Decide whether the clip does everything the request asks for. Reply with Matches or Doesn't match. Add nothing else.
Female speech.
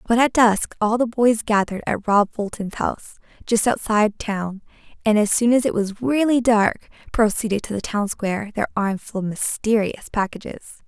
Matches